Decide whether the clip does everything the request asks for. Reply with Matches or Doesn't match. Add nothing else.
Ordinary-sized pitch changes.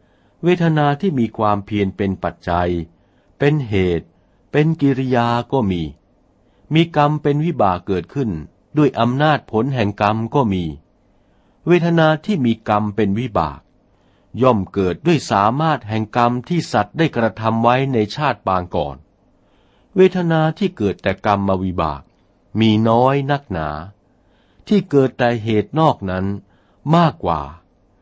Doesn't match